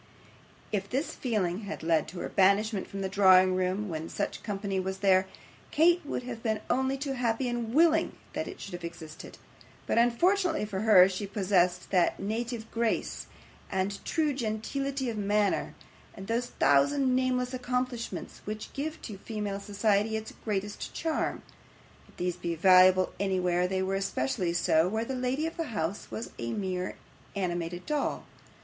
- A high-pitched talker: Yes, high, 205 Hz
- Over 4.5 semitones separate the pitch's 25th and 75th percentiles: Yes, average, 4.9 semitones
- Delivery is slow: No, average, 165 wpm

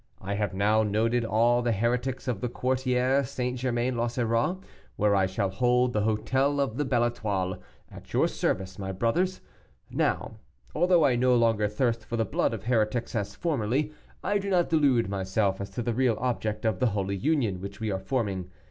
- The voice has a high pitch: No, low, 115 Hz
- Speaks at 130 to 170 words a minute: No, average, 190 wpm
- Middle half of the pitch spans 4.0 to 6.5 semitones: No, average, 3.6 semitones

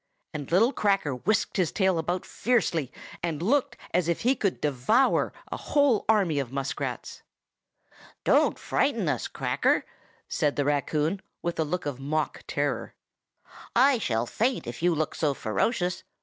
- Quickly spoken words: No, average, 150 wpm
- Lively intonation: Yes, wide, 6.7 semitones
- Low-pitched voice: No, medium, 170 Hz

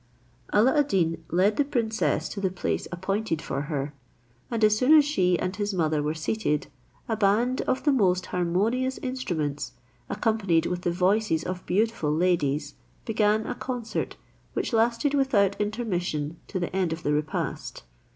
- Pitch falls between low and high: No, high, 195 Hz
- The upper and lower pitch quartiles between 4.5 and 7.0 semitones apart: Yes, average, 5.0 semitones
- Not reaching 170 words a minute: Yes, average, 160 wpm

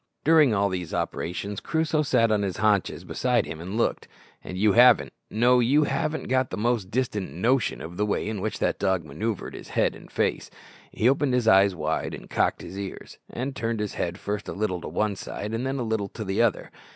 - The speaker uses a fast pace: Yes, fast, 220 wpm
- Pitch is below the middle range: Yes, low, 110 Hz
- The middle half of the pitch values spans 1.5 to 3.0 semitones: No, average, 4.2 semitones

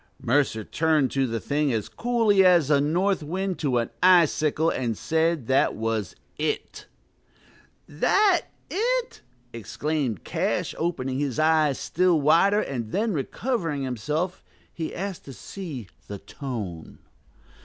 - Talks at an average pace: No, slow, 130 wpm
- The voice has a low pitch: No, medium, 150 Hz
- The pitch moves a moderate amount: No, wide, 5.9 semitones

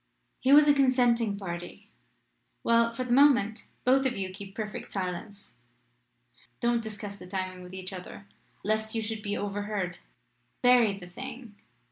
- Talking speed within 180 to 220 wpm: No, average, 150 wpm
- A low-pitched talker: No, high, 210 Hz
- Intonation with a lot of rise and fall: No, average, 3.7 semitones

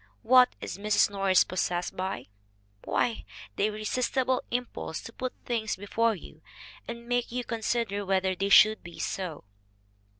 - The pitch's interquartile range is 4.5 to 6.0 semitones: No, average, 3.9 semitones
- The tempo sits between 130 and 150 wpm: Yes, average, 145 wpm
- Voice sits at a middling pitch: No, high, 215 Hz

